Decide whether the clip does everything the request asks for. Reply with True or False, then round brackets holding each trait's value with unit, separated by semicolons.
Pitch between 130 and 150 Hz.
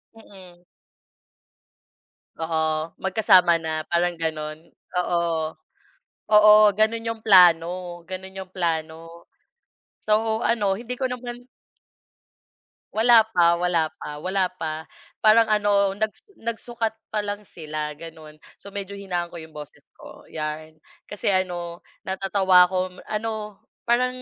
False (190 Hz)